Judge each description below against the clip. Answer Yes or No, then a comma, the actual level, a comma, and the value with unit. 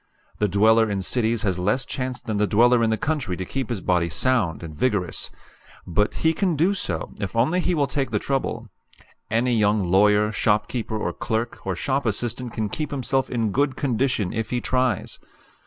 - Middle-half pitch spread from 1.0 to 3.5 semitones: No, average, 3.9 semitones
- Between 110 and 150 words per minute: No, average, 190 wpm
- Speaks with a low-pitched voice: Yes, low, 115 Hz